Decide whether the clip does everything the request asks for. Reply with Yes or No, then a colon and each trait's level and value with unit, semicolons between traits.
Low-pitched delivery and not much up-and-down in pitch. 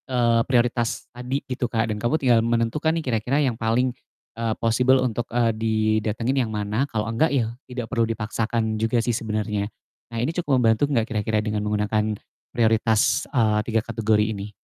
Yes: low, 115 Hz; narrow, 2.1 semitones